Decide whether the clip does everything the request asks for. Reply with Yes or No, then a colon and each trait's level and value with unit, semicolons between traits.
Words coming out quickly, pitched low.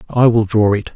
Yes: fast, 250 wpm; low, 110 Hz